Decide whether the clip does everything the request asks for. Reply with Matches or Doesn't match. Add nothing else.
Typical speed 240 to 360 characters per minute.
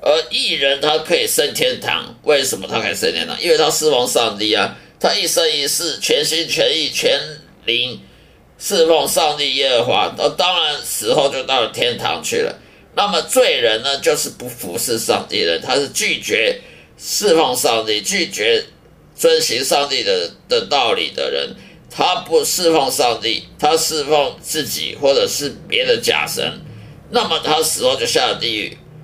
Matches